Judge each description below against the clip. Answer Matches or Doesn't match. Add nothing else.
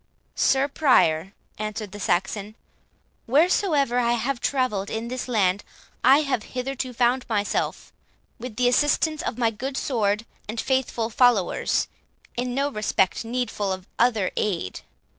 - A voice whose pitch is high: Matches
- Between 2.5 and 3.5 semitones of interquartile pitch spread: Doesn't match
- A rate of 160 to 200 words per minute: Doesn't match